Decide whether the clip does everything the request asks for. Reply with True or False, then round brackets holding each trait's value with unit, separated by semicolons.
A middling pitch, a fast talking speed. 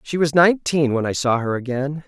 True (145 Hz; 230 wpm)